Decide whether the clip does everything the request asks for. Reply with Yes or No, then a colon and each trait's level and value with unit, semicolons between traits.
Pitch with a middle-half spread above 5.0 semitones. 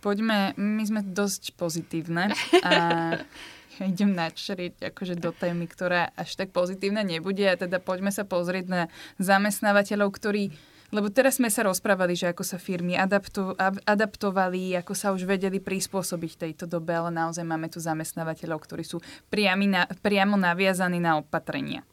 No: average, 2.7 semitones